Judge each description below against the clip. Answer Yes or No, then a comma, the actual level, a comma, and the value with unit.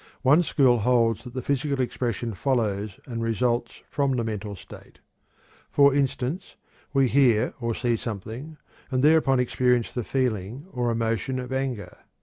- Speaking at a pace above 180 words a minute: No, average, 145 wpm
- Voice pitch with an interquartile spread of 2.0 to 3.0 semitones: Yes, average, 2.7 semitones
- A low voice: Yes, low, 125 Hz